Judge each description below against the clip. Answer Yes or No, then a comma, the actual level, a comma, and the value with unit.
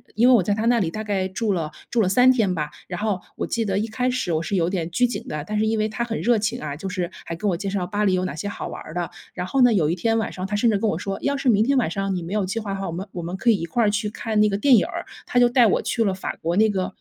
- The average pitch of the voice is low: No, high, 205 Hz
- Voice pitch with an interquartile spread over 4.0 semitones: No, average, 3.7 semitones